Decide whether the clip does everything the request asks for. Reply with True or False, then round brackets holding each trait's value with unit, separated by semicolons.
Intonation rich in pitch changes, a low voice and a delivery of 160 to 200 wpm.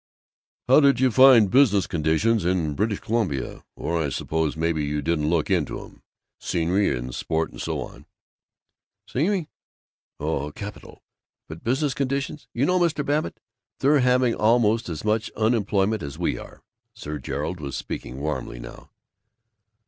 False (8.3 semitones; 100 Hz; 150 wpm)